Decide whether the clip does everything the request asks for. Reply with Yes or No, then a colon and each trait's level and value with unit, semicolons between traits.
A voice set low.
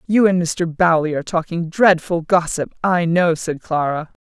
No: medium, 170 Hz